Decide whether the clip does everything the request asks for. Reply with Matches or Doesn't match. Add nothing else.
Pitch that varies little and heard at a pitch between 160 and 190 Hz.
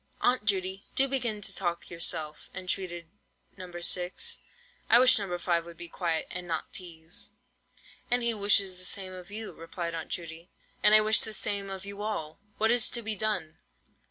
Doesn't match